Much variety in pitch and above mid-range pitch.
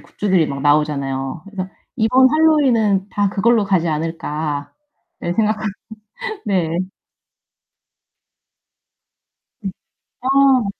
Yes: wide, 6.2 semitones; high, 195 Hz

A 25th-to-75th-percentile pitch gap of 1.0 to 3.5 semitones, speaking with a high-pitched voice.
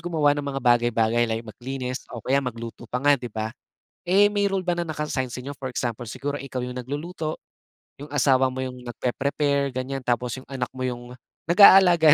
No: average, 3.2 semitones; low, 130 Hz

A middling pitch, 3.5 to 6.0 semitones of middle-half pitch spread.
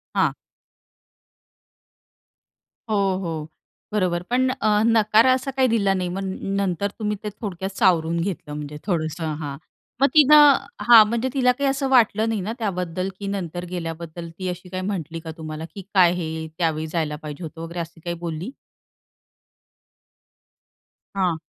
Yes: medium, 180 Hz; average, 4.7 semitones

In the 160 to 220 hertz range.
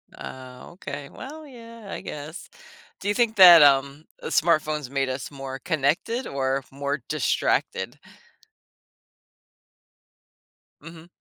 No: medium, 150 Hz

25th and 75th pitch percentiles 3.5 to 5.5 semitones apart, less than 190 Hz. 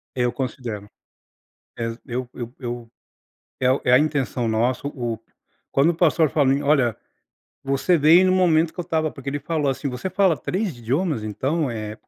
Yes: average, 4.6 semitones; low, 135 Hz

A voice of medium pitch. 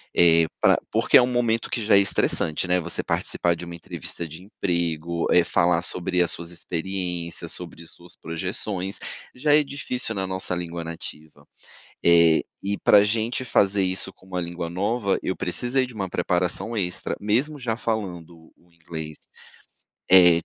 No: very low, 90 Hz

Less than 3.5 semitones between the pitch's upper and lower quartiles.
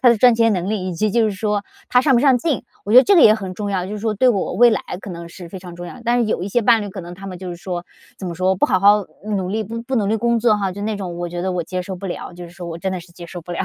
No: average, 3.8 semitones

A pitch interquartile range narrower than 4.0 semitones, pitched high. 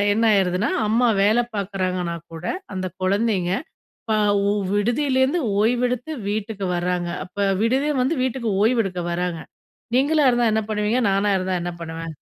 No: average, 4.8 semitones; high, 210 Hz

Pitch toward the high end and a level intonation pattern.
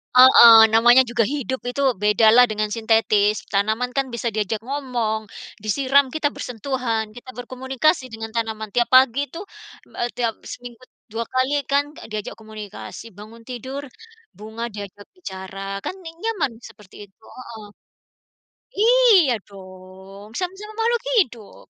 No: high, 235 Hz; average, 3.8 semitones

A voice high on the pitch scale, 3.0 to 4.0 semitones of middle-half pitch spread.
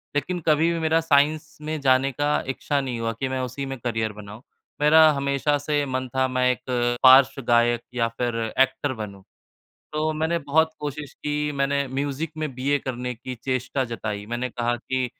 No: low, 135 Hz; average, 3.3 semitones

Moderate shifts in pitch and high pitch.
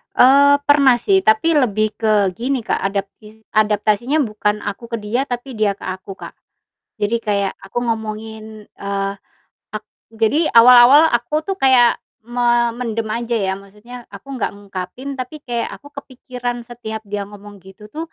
Yes: average, 3.1 semitones; high, 225 Hz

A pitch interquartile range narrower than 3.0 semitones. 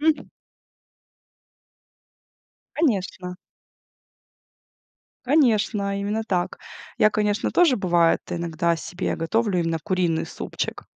No: average, 4.4 semitones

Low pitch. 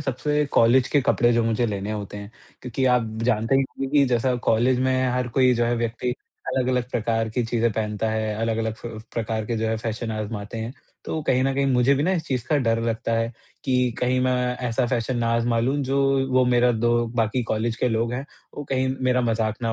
Yes: low, 120 Hz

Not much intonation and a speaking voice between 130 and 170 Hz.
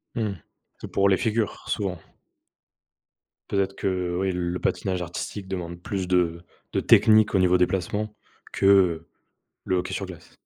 No: narrow, 1.9 semitones; very low, 95 Hz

